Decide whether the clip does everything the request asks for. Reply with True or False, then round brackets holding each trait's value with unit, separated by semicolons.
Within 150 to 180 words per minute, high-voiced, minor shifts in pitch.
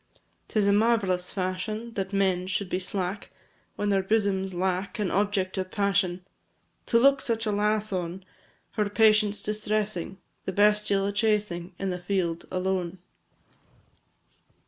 False (140 wpm; 200 Hz; 2.2 semitones)